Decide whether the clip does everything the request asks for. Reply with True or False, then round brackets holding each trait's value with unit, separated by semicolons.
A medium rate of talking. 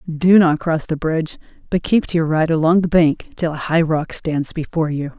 False (230 wpm)